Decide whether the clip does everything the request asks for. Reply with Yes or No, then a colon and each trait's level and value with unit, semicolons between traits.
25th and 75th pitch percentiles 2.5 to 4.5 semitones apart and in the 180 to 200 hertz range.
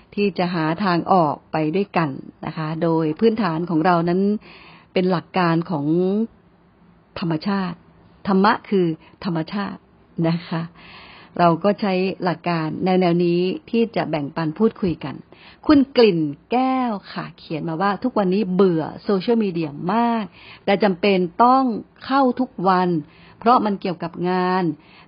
Yes: average, 3.6 semitones; medium, 185 Hz